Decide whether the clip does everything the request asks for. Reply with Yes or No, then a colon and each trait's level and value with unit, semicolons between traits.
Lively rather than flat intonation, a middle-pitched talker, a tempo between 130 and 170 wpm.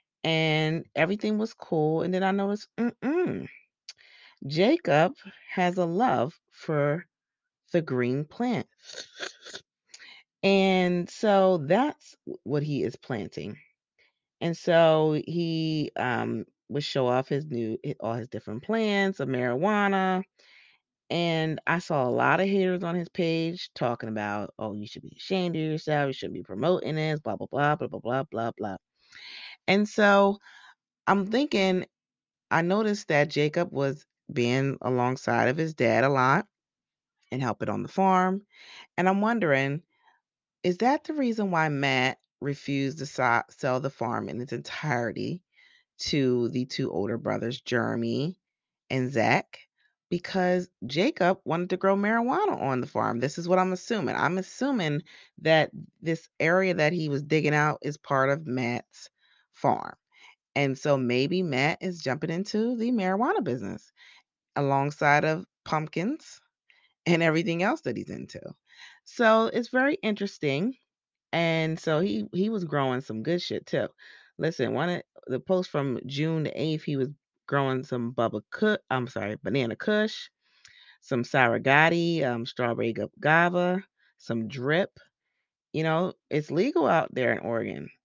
Yes: wide, 6.3 semitones; medium, 160 Hz; average, 145 wpm